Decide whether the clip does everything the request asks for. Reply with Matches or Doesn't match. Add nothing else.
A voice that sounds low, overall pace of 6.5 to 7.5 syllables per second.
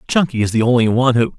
Matches